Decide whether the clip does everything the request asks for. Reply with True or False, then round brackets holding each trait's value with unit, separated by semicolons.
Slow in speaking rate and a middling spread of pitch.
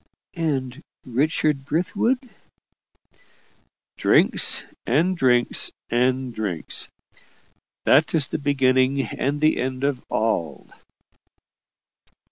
True (85 wpm; 3.1 semitones)